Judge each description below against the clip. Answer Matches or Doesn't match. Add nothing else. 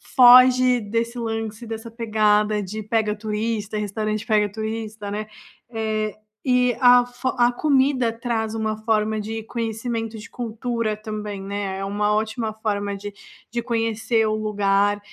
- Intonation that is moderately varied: Doesn't match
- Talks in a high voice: Matches